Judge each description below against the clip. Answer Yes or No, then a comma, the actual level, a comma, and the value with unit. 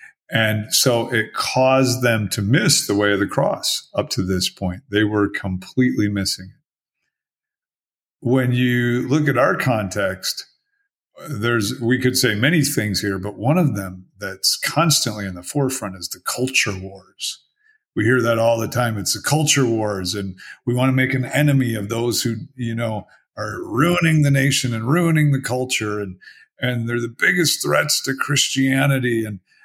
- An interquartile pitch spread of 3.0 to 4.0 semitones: No, average, 4.6 semitones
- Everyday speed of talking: Yes, average, 175 wpm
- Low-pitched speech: Yes, low, 120 Hz